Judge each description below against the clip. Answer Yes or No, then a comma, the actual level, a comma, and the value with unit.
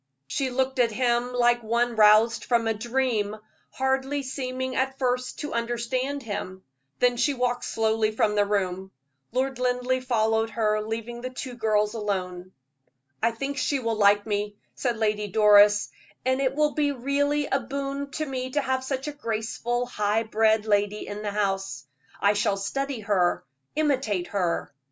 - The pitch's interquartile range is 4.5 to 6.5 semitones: No, average, 3.7 semitones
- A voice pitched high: Yes, high, 235 Hz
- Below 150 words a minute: No, average, 165 wpm